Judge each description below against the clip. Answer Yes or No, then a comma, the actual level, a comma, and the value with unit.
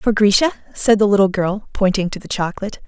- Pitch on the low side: No, high, 200 Hz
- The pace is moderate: No, fast, 210 wpm